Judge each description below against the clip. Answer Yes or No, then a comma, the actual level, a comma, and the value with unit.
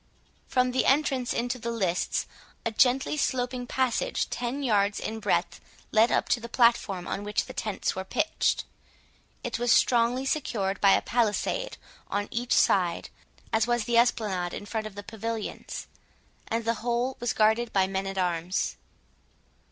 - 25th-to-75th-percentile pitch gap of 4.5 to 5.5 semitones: No, average, 3.2 semitones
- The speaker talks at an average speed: Yes, average, 160 wpm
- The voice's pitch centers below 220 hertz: No, high, 230 Hz